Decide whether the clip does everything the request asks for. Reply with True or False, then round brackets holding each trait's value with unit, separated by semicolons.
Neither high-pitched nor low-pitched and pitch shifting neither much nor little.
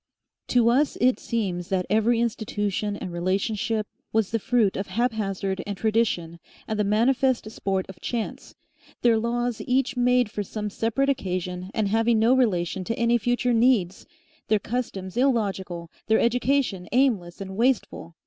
False (220 Hz; 3.9 semitones)